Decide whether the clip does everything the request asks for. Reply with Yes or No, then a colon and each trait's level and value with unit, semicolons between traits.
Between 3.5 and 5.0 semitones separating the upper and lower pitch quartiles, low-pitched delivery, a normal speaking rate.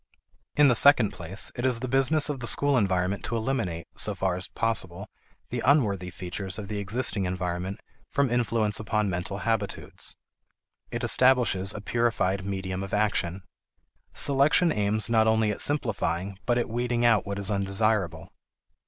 Yes: average, 4.0 semitones; low, 105 Hz; average, 160 wpm